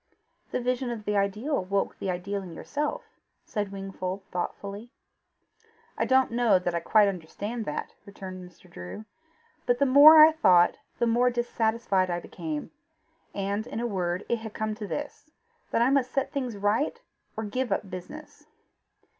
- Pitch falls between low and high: No, high, 215 Hz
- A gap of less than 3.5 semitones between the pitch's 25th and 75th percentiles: No, average, 4.3 semitones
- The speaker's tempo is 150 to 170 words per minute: Yes, average, 165 wpm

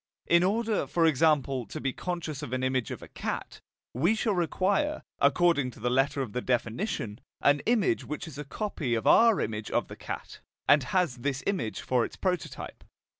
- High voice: No, medium, 150 Hz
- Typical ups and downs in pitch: No, wide, 6.2 semitones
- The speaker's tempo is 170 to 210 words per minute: Yes, average, 190 wpm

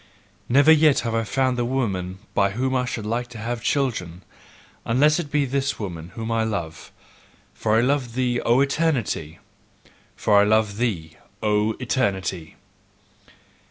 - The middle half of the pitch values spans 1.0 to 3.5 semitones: No, average, 4.4 semitones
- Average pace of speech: Yes, average, 155 wpm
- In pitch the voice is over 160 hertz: No, low, 115 Hz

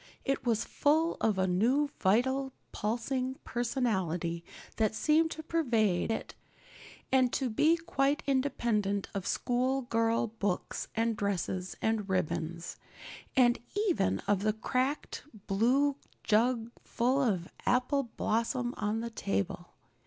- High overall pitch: Yes, high, 230 Hz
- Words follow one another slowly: Yes, slow, 120 wpm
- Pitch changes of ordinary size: Yes, average, 4.6 semitones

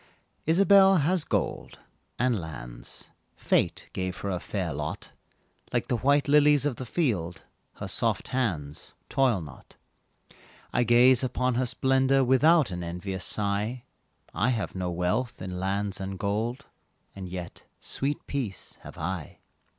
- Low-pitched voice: Yes, low, 110 Hz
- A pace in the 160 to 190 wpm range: No, average, 140 wpm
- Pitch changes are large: Yes, wide, 6.3 semitones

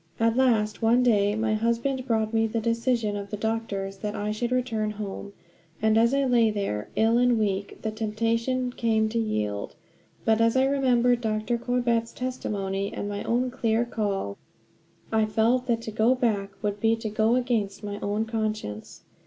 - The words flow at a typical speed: Yes, average, 180 wpm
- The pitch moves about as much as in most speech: No, narrow, 2.2 semitones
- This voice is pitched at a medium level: No, high, 225 Hz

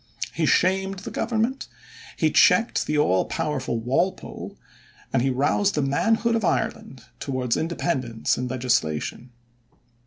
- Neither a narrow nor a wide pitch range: No, wide, 7.6 semitones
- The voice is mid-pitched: Yes, medium, 150 Hz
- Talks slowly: Yes, slow, 125 wpm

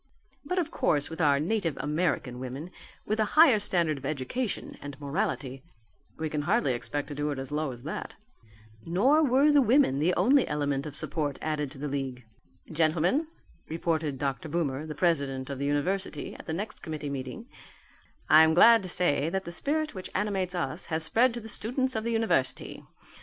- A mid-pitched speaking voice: Yes, medium, 160 Hz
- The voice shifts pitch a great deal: Yes, wide, 6.5 semitones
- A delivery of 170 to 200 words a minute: Yes, average, 190 wpm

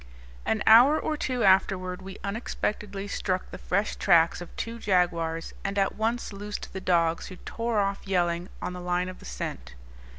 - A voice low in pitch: No, high, 195 Hz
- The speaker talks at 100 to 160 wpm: No, average, 175 wpm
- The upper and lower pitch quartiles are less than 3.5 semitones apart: Yes, average, 2.9 semitones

